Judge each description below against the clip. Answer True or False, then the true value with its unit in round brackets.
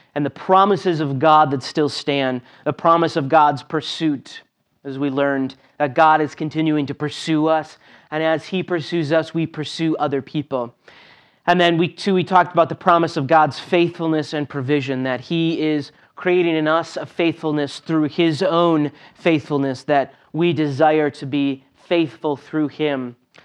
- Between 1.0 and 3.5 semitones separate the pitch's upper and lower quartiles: True (2.5 semitones)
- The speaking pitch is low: False (155 Hz)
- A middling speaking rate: True (170 wpm)